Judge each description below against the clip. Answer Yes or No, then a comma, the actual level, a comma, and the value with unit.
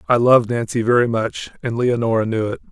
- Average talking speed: Yes, average, 175 wpm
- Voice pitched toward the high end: No, low, 115 Hz